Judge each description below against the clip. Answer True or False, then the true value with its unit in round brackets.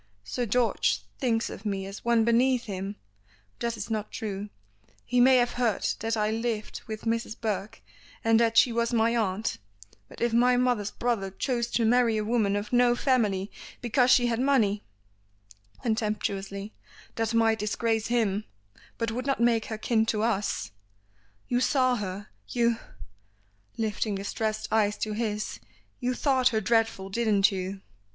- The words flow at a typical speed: True (160 wpm)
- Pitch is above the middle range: True (225 Hz)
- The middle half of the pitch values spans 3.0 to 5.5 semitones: False (2.5 semitones)